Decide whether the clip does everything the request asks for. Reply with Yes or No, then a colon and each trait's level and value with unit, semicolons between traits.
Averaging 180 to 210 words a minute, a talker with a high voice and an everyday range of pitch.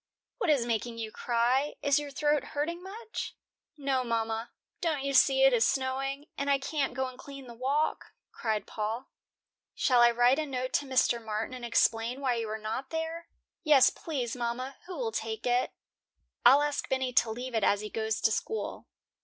Yes: average, 190 wpm; very high, 255 Hz; average, 3.3 semitones